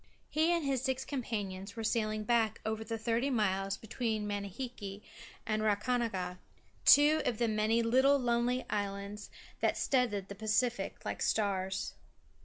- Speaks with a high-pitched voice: Yes, high, 220 Hz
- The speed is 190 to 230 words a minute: No, average, 145 wpm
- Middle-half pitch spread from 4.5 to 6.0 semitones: No, average, 3.4 semitones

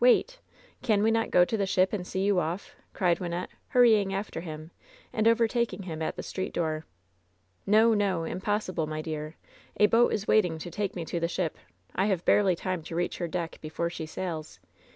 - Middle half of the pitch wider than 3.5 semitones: Yes, average, 3.9 semitones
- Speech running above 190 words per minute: Yes, average, 200 wpm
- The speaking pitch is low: No, medium, 185 Hz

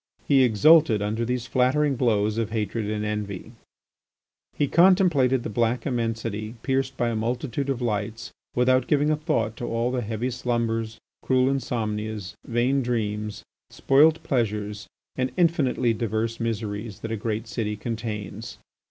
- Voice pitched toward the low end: Yes, low, 115 Hz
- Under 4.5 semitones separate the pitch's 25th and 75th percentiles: Yes, average, 3.0 semitones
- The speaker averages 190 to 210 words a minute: No, average, 145 wpm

